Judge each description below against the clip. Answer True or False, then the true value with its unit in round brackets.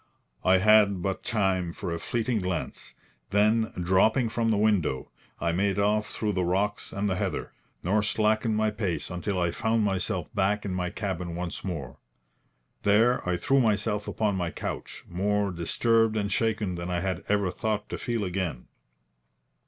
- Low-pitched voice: True (100 Hz)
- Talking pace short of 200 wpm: True (170 wpm)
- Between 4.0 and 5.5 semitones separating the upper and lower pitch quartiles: False (3.0 semitones)